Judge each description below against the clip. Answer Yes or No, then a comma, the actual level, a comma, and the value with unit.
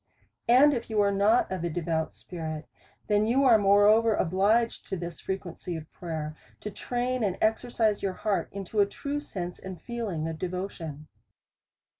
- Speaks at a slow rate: No, average, 165 wpm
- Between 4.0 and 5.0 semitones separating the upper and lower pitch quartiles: Yes, average, 4.5 semitones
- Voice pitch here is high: Yes, high, 200 Hz